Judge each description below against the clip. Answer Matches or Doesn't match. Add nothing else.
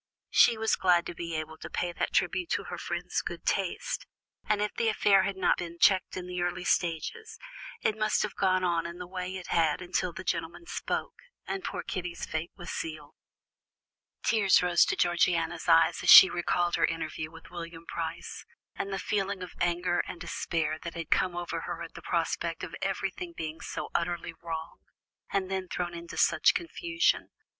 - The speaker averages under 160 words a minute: Doesn't match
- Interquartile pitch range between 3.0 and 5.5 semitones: Doesn't match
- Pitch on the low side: Doesn't match